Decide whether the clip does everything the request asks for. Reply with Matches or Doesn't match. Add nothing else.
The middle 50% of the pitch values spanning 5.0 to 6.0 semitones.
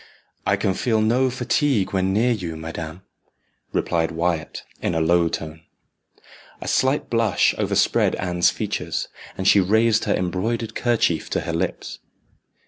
Matches